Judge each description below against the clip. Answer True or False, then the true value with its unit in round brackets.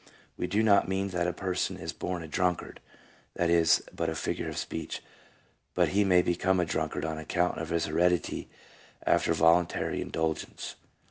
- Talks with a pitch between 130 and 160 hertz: False (85 Hz)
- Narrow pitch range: True (2.0 semitones)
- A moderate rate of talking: True (180 wpm)